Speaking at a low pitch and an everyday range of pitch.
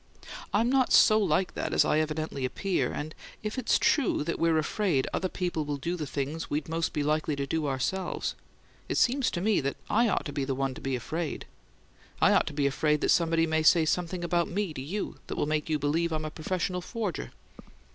No: medium, 160 Hz; average, 3.8 semitones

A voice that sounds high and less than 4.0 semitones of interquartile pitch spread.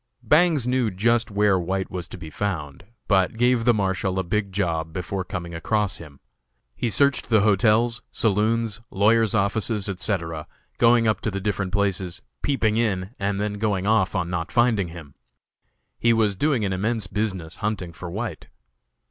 No: low, 100 Hz; average, 3.4 semitones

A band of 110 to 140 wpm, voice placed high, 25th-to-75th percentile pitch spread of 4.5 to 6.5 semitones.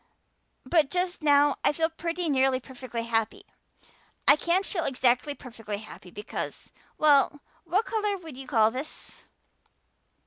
Yes: slow, 135 wpm; very high, 285 Hz; average, 5.1 semitones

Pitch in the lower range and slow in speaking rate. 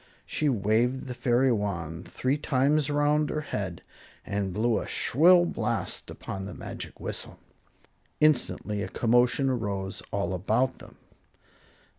Yes: low, 120 Hz; slow, 130 wpm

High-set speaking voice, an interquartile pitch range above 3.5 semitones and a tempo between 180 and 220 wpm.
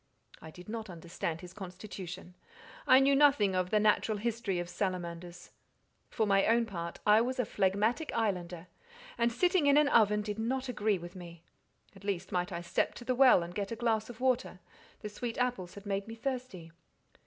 Yes: high, 210 Hz; average, 4.8 semitones; average, 190 wpm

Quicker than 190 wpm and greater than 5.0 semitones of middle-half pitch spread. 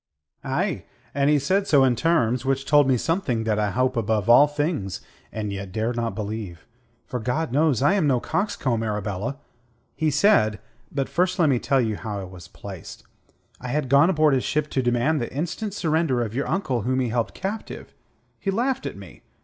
Yes: average, 200 wpm; wide, 5.6 semitones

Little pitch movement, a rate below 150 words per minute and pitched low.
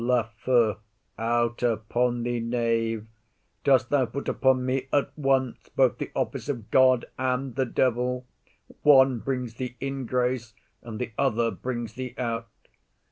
Yes: narrow, 2.0 semitones; average, 140 wpm; low, 125 Hz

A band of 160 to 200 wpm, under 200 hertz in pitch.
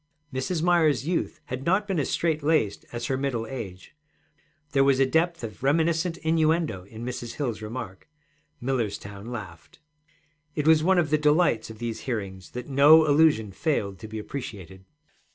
Yes: average, 165 wpm; low, 135 Hz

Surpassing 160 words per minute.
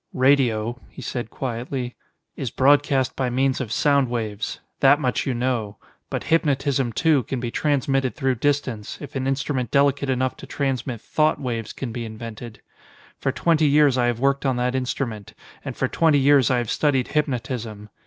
Yes: average, 175 wpm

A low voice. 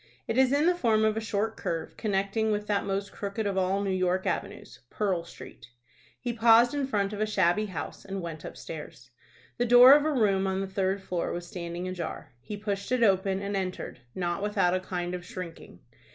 No: high, 195 Hz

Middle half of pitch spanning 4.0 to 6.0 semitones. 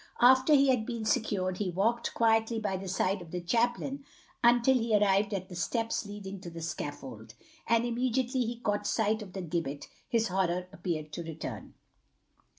Yes: average, 4.6 semitones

